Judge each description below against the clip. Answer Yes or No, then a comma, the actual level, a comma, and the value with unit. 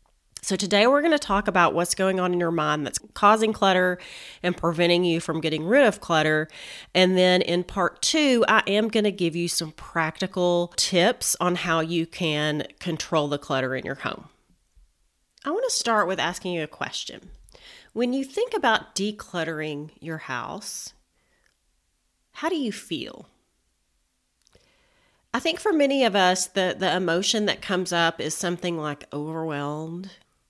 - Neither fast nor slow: Yes, average, 165 wpm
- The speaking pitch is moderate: Yes, medium, 175 Hz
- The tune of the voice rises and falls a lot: No, average, 4.6 semitones